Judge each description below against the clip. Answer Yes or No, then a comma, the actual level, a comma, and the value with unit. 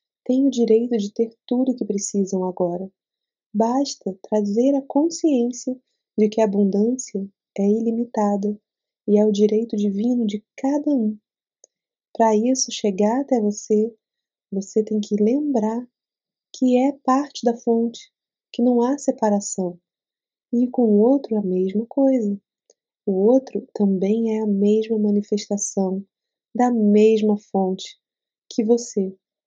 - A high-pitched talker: Yes, high, 220 Hz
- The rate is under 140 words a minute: Yes, average, 130 wpm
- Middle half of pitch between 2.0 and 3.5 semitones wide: Yes, average, 3.2 semitones